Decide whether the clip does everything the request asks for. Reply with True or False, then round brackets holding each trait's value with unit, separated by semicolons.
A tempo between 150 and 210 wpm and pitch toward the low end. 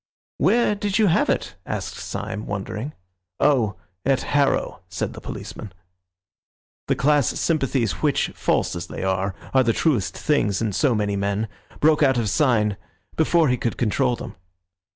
True (155 wpm; 125 Hz)